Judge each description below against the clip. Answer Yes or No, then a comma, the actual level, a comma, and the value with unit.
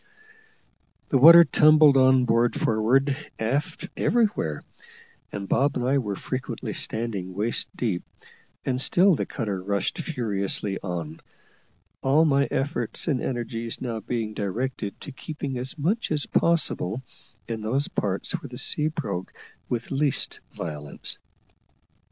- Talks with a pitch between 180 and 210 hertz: No, low, 125 Hz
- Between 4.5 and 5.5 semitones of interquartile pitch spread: Yes, average, 5.1 semitones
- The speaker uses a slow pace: Yes, slow, 130 wpm